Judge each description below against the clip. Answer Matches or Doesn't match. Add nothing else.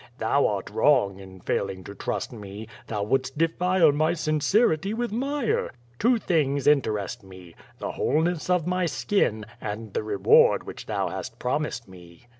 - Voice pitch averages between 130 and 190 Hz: Matches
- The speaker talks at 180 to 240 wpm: Doesn't match